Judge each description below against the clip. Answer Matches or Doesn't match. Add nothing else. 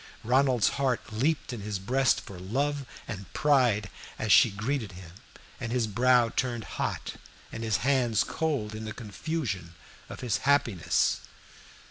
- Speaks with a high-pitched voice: Doesn't match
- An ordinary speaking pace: Matches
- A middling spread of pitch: Matches